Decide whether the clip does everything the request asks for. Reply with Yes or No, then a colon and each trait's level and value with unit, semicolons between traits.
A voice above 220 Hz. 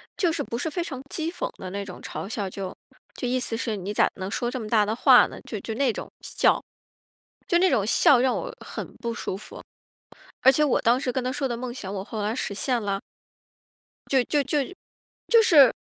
Yes: high, 240 Hz